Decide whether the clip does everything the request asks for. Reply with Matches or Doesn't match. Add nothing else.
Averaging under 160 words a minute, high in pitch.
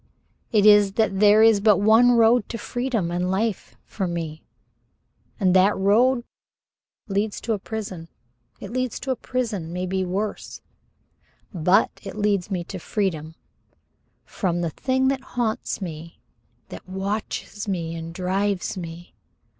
Matches